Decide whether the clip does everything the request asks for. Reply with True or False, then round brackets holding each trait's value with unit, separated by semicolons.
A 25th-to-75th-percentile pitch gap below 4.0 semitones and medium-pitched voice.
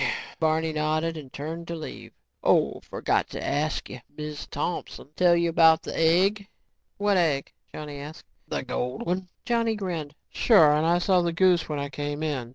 True (2.8 semitones; 160 Hz)